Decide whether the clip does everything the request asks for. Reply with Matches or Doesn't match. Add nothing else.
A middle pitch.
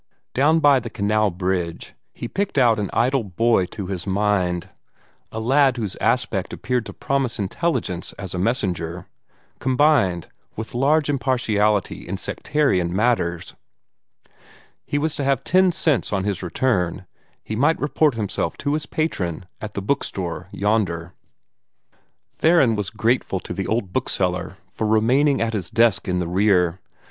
Doesn't match